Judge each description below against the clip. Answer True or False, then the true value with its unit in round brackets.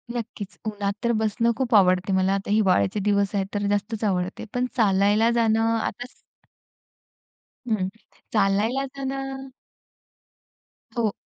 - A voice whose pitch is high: True (210 Hz)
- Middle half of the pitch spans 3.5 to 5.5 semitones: False (2.8 semitones)